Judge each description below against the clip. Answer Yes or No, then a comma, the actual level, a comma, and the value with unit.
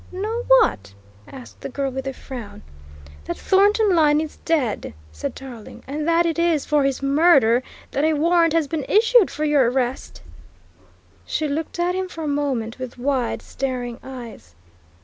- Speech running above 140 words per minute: Yes, average, 170 wpm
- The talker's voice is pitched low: No, very high, 285 Hz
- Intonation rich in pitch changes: No, average, 4.7 semitones